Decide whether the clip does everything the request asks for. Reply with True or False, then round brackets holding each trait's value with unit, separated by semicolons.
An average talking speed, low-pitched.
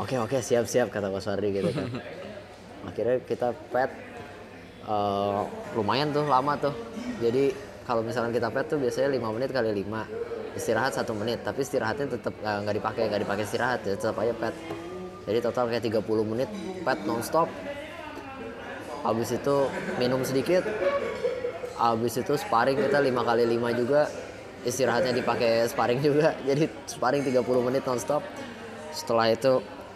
False (150 wpm; 125 Hz)